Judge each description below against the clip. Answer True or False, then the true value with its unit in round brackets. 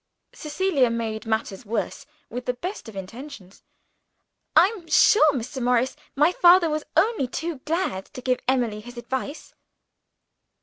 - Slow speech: True (130 wpm)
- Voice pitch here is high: True (260 Hz)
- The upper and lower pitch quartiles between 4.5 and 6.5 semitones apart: True (5.4 semitones)